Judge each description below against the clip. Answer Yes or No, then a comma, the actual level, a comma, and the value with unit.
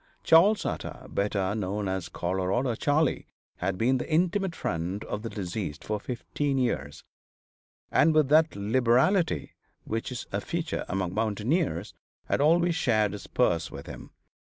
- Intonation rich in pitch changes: Yes, wide, 8.0 semitones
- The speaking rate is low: No, average, 145 wpm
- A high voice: No, low, 115 Hz